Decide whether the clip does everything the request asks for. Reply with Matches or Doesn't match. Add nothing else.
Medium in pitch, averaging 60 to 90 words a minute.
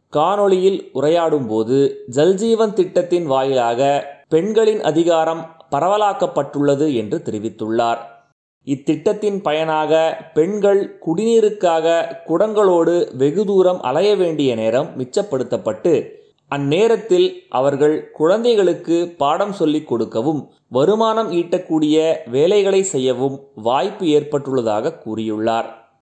Matches